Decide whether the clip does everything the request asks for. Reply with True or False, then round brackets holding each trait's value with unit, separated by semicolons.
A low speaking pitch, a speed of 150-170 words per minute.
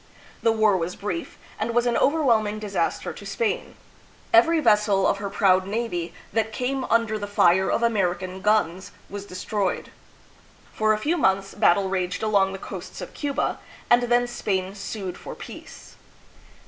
False (210 Hz; 160 wpm)